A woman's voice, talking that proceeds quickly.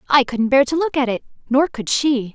Yes: female; fast, 230 wpm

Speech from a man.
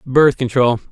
Yes: male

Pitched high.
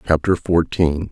No: very low, 85 Hz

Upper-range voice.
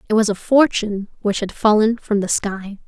Yes: high, 210 Hz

